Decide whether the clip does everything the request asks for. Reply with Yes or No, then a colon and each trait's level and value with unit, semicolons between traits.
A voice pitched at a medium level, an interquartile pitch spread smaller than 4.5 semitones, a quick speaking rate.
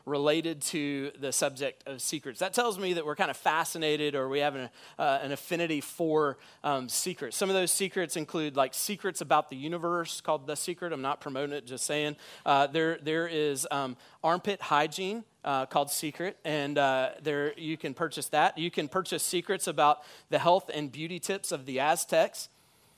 No: medium, 155 Hz; average, 3.2 semitones; average, 190 wpm